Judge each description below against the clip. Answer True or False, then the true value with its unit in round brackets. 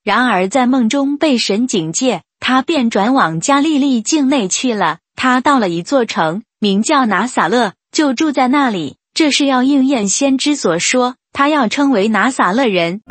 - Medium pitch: False (255 Hz)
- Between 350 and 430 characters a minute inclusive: False (245 characters per minute)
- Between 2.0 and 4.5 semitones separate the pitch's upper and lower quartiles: False (5.4 semitones)